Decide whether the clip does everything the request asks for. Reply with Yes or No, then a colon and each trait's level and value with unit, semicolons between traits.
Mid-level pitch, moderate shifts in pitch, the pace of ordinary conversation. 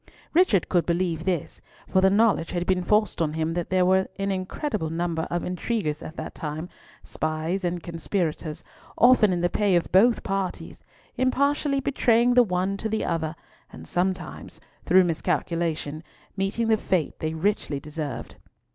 Yes: medium, 180 Hz; average, 4.0 semitones; average, 160 wpm